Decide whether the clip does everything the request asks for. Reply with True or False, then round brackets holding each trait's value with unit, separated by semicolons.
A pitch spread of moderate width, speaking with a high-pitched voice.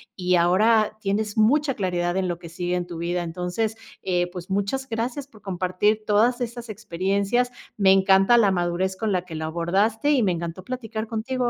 True (4.0 semitones; 195 Hz)